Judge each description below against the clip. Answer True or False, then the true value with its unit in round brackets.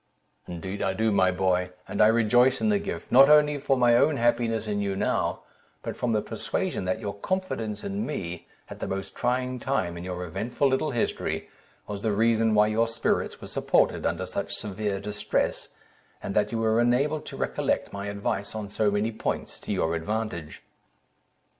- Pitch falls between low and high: False (110 Hz)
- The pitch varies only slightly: False (3.7 semitones)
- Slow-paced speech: False (185 wpm)